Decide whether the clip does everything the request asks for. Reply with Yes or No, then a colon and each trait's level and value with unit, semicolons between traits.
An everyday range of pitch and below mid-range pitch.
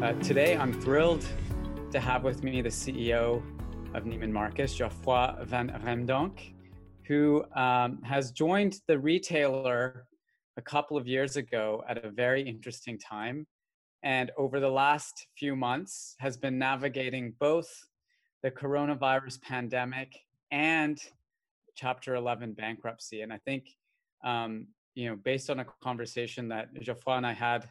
Yes: average, 3.2 semitones; low, 130 Hz